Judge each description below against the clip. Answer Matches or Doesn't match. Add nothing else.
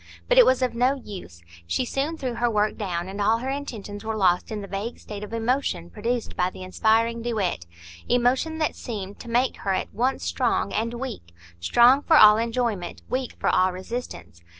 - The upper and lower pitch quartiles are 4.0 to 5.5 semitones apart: Matches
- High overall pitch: Matches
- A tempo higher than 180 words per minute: Matches